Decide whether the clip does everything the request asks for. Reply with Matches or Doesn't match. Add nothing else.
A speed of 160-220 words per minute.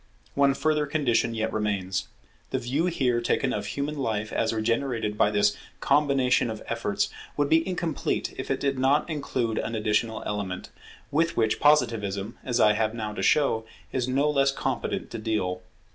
Matches